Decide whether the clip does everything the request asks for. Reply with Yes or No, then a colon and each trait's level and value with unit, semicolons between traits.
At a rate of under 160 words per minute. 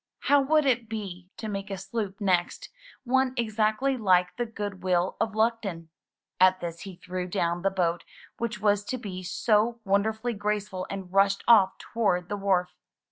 No: average, 175 wpm